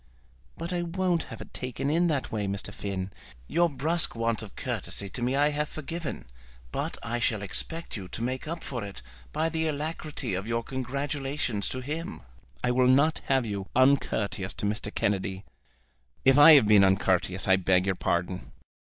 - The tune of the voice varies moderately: No, wide, 6.9 semitones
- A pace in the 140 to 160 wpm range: No, average, 180 wpm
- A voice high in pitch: No, low, 125 Hz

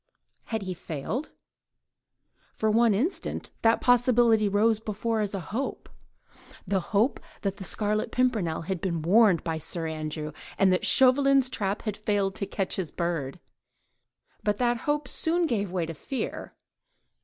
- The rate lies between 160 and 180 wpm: No, average, 150 wpm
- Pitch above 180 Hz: Yes, high, 210 Hz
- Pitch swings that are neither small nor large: Yes, average, 4.6 semitones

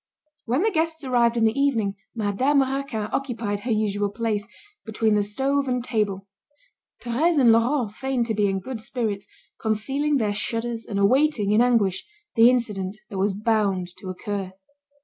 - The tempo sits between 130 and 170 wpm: Yes, average, 165 wpm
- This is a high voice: Yes, high, 225 Hz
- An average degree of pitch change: Yes, average, 4.0 semitones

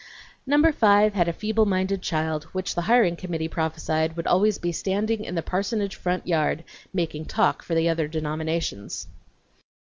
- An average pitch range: Yes, average, 4.1 semitones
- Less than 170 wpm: Yes, average, 160 wpm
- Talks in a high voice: No, medium, 175 Hz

